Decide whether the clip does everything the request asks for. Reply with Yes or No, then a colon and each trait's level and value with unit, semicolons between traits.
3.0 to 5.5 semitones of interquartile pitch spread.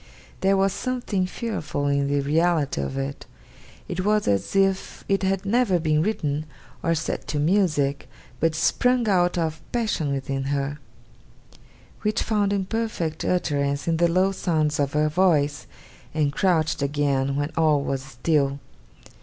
Yes: average, 5.1 semitones